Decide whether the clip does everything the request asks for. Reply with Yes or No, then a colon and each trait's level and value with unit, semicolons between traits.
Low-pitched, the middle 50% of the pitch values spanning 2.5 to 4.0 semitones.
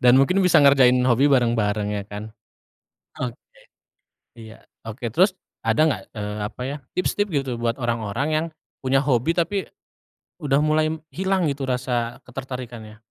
No: low, 125 Hz; average, 4.8 semitones